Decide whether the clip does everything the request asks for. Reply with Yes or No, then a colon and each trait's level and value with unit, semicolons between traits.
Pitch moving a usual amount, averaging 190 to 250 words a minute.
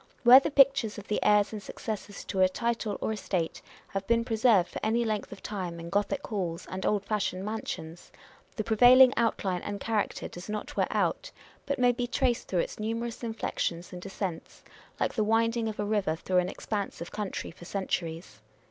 Yes: average, 3.5 semitones; average, 195 wpm